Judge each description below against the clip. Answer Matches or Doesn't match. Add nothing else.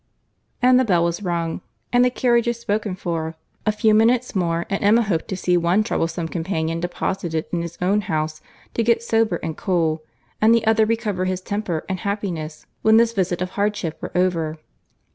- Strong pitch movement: Doesn't match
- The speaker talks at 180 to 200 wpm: Matches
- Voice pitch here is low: Doesn't match